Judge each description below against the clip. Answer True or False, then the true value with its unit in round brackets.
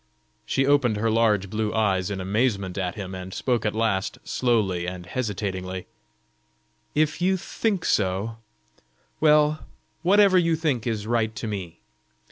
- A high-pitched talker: False (110 Hz)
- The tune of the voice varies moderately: False (5.9 semitones)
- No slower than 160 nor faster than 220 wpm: False (140 wpm)